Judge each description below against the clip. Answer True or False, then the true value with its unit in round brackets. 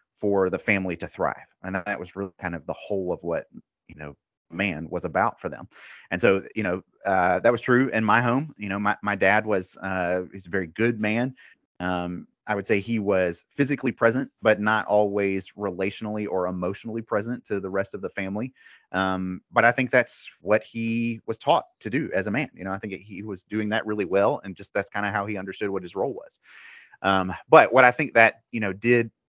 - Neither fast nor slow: False (230 wpm)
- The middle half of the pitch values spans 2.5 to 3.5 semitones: True (3.1 semitones)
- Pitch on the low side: True (105 Hz)